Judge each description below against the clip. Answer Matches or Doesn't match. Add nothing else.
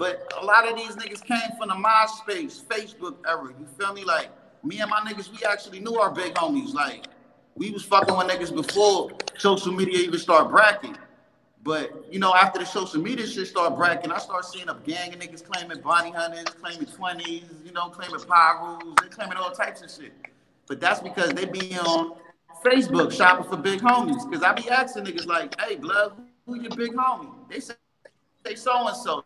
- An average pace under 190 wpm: Doesn't match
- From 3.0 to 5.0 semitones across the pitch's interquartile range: Doesn't match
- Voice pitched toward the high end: Matches